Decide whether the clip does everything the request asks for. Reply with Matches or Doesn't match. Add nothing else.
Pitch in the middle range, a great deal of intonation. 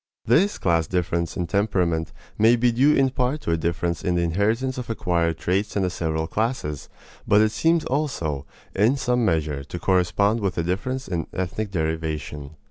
Doesn't match